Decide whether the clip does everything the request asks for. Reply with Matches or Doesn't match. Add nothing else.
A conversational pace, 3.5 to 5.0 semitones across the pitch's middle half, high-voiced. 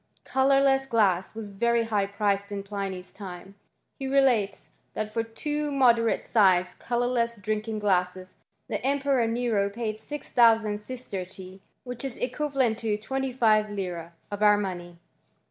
Doesn't match